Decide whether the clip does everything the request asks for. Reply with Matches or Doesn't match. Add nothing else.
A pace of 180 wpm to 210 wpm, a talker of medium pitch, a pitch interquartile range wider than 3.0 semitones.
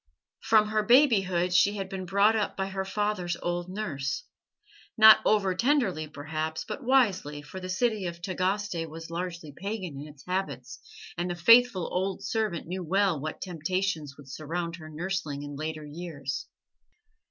Doesn't match